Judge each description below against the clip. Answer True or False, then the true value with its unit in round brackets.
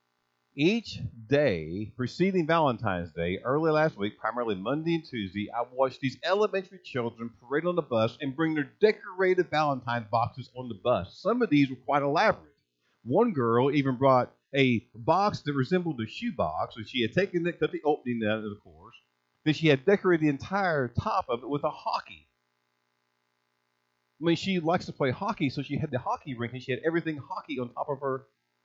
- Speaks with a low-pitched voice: True (130 Hz)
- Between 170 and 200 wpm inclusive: True (195 wpm)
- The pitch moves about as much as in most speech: False (6.5 semitones)